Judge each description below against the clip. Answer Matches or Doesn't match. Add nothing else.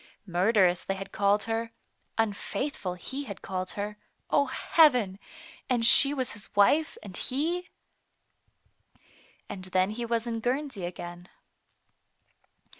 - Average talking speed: Doesn't match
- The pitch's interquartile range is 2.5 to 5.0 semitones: Doesn't match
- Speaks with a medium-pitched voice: Doesn't match